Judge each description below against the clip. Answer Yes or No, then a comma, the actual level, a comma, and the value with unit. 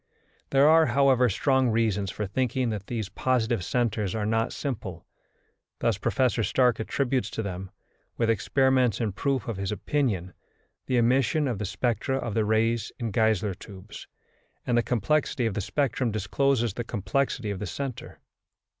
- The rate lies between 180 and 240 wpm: No, average, 160 wpm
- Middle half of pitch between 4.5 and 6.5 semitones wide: No, average, 3.8 semitones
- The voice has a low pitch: Yes, low, 115 Hz